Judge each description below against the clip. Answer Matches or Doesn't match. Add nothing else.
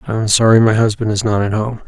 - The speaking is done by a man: Matches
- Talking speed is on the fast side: Matches